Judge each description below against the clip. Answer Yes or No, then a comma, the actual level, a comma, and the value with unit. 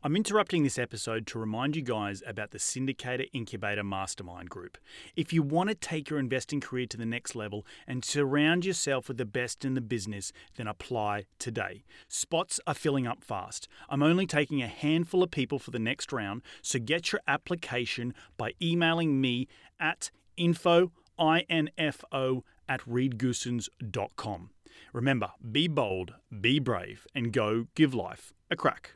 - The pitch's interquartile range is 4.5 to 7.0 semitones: Yes, average, 5.0 semitones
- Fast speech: No, average, 160 wpm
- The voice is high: No, low, 130 Hz